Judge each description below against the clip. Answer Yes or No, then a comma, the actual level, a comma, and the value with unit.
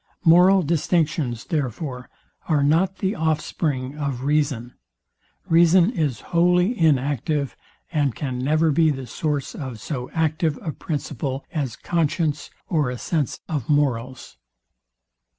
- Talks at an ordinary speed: No, slow, 120 wpm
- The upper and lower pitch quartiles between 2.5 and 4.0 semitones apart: Yes, average, 3.5 semitones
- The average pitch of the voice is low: No, medium, 150 Hz